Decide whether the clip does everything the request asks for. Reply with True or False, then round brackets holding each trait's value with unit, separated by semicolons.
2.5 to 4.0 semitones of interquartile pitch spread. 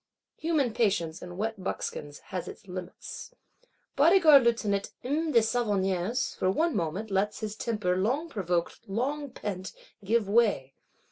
False (4.9 semitones)